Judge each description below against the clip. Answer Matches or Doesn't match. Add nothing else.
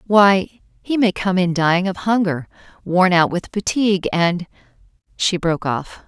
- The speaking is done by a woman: Matches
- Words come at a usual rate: Matches